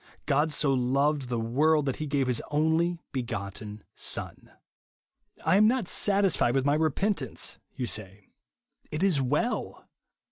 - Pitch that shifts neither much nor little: Yes, average, 4.5 semitones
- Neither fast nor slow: Yes, average, 150 wpm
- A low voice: No, medium, 145 Hz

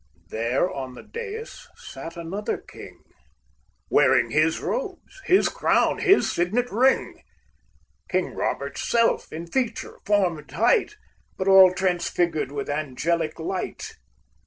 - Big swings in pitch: Yes, wide, 7.9 semitones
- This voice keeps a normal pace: No, slow, 120 wpm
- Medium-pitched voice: Yes, medium, 180 Hz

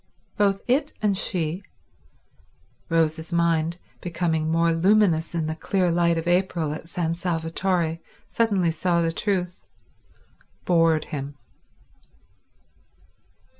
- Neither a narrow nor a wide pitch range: No, narrow, 2.2 semitones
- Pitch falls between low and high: Yes, medium, 170 Hz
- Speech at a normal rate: No, slow, 95 wpm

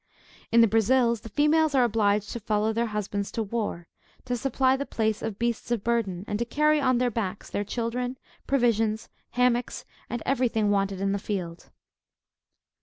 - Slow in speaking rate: No, average, 180 wpm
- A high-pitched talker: Yes, high, 230 Hz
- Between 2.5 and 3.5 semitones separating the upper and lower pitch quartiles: Yes, average, 3.1 semitones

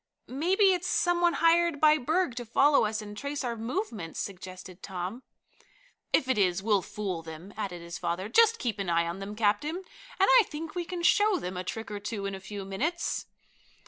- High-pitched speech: Yes, high, 220 Hz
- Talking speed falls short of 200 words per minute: No, fast, 205 wpm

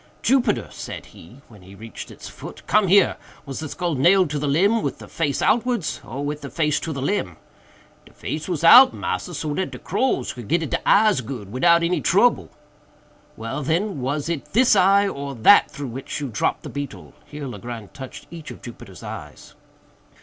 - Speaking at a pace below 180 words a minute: No, average, 195 wpm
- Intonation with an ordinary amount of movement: No, wide, 5.8 semitones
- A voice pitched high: No, medium, 150 Hz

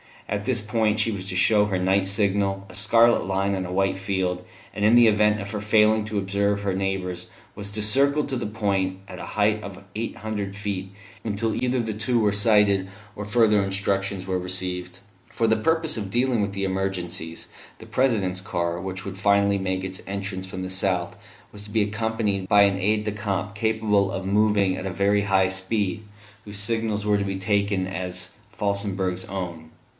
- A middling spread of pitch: No, narrow, 1.9 semitones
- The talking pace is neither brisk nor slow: Yes, average, 195 wpm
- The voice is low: Yes, low, 100 Hz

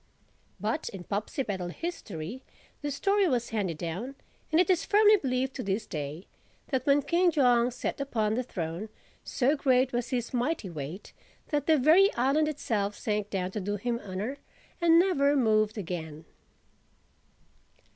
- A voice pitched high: Yes, high, 240 Hz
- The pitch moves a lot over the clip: Yes, wide, 6.4 semitones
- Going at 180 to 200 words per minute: No, average, 155 wpm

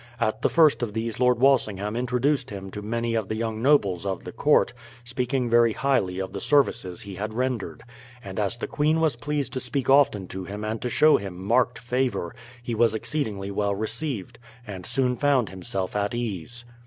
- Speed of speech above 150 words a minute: Yes, average, 195 wpm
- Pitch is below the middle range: Yes, low, 115 Hz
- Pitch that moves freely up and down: No, average, 4.0 semitones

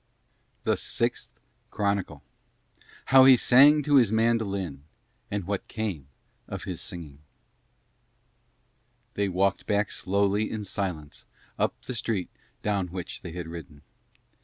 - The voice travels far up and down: No, average, 4.0 semitones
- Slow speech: Yes, slow, 120 wpm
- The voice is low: Yes, low, 100 Hz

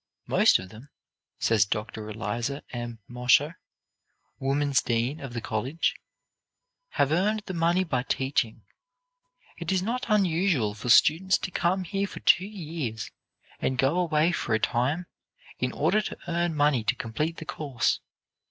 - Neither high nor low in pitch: Yes, medium, 145 Hz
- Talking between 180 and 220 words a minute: No, average, 150 wpm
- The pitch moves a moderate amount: No, wide, 6.5 semitones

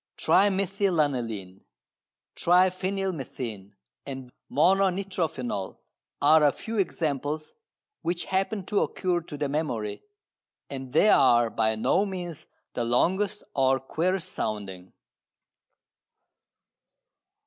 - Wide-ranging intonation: Yes, wide, 7.2 semitones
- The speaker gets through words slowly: Yes, slow, 90 wpm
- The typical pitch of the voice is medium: Yes, medium, 155 Hz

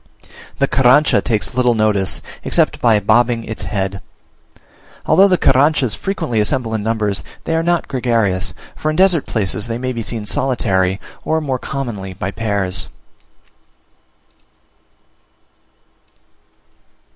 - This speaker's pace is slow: Yes, slow, 120 wpm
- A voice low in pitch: Yes, low, 115 Hz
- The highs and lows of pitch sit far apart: No, average, 4.8 semitones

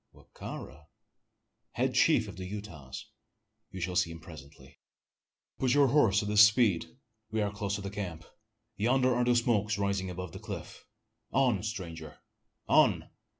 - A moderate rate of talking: Yes, average, 160 wpm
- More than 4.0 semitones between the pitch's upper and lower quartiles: Yes, average, 4.4 semitones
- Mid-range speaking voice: No, low, 100 Hz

